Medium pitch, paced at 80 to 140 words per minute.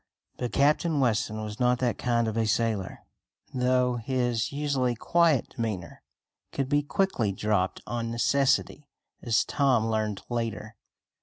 No: low, 120 Hz; slow, 135 wpm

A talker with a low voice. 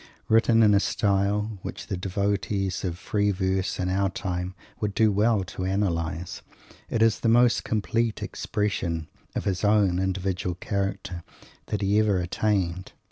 Yes: low, 100 Hz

